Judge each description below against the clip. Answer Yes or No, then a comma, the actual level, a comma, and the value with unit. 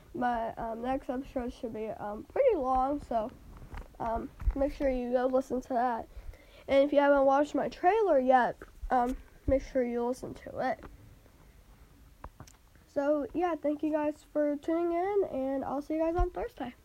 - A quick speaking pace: No, average, 170 wpm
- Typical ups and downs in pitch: Yes, average, 3.1 semitones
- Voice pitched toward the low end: No, very high, 270 Hz